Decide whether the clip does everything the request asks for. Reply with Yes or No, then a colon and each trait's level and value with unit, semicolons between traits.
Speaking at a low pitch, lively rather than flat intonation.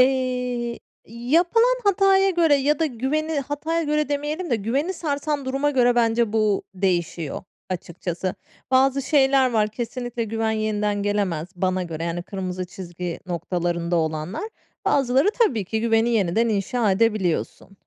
No: high, 235 Hz; wide, 6.8 semitones